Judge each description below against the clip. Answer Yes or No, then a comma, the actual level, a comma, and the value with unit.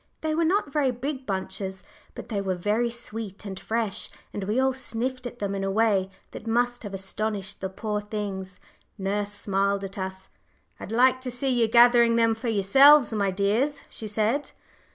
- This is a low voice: No, high, 220 Hz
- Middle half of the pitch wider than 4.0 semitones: No, average, 3.7 semitones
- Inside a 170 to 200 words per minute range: Yes, average, 185 wpm